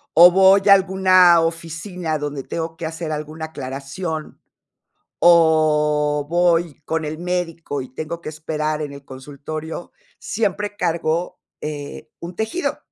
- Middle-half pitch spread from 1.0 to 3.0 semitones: Yes, narrow, 2.6 semitones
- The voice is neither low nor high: Yes, medium, 160 Hz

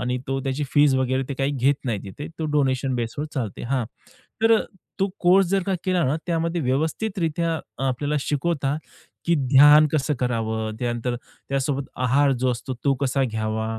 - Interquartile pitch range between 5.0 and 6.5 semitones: No, average, 3.5 semitones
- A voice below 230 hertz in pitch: Yes, low, 135 Hz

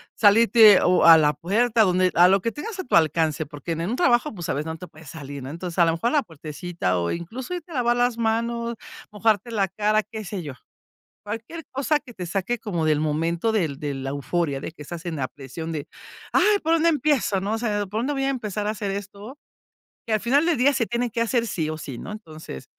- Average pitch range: No, wide, 6.5 semitones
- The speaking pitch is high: Yes, high, 205 Hz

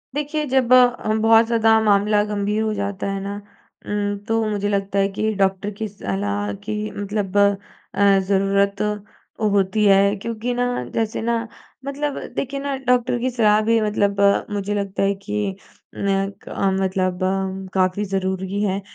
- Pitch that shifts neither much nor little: No, narrow, 2.3 semitones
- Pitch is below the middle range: No, high, 205 Hz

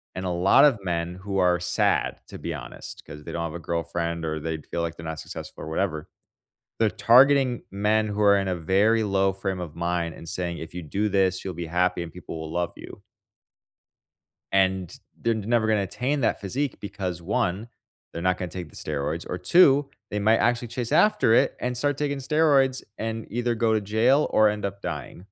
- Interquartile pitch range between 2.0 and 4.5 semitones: No, average, 4.9 semitones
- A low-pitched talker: Yes, very low, 95 Hz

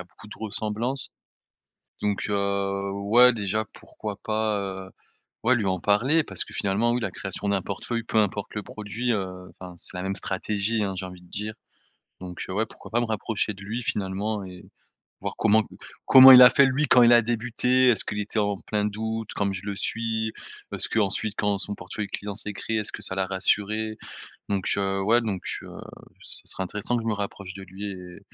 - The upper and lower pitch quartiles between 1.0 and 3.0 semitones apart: Yes, narrow, 2.4 semitones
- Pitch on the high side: No, low, 105 Hz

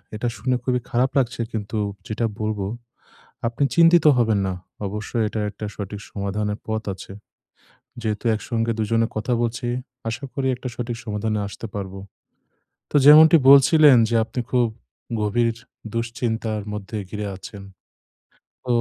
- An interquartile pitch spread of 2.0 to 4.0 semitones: Yes, average, 2.7 semitones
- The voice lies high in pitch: No, low, 115 Hz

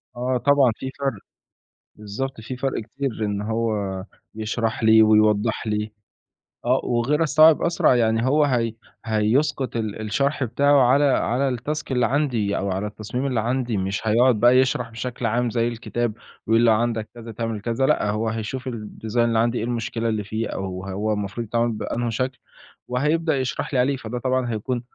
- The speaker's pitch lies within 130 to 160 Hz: No, low, 115 Hz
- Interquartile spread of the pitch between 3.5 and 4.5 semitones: No, average, 3.0 semitones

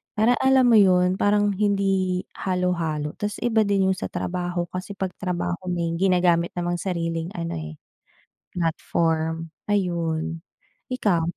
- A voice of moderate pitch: Yes, medium, 180 Hz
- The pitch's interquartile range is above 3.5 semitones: No, average, 2.8 semitones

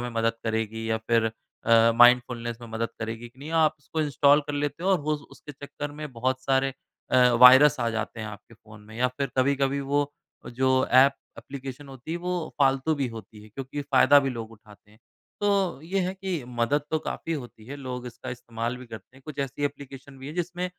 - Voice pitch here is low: Yes, low, 130 Hz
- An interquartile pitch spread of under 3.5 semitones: No, average, 3.8 semitones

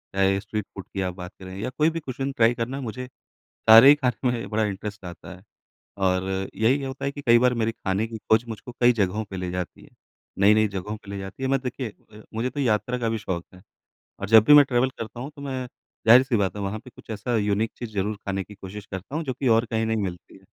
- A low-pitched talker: Yes, low, 110 Hz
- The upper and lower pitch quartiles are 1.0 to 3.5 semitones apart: No, average, 4.1 semitones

